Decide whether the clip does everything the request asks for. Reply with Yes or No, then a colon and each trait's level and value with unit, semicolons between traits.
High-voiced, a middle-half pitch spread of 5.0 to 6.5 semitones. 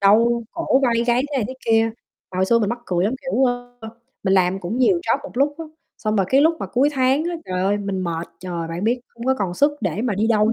Yes: high, 225 Hz; average, 5.3 semitones